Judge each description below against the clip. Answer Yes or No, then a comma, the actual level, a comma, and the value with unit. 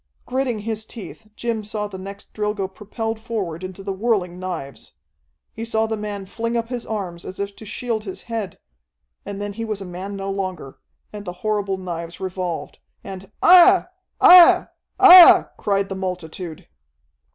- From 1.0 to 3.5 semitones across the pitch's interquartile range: Yes, average, 3.0 semitones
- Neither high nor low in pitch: No, high, 200 Hz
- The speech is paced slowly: No, average, 165 wpm